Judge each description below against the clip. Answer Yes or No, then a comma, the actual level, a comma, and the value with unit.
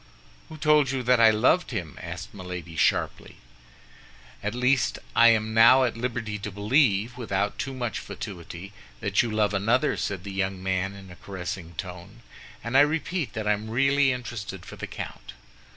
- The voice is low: Yes, low, 110 Hz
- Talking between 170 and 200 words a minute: Yes, average, 175 wpm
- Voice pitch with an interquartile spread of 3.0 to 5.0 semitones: Yes, average, 4.5 semitones